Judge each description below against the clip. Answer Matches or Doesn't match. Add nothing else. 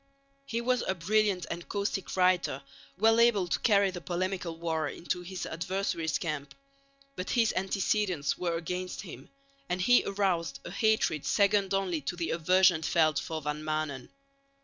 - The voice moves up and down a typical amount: Matches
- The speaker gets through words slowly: Doesn't match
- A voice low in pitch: Doesn't match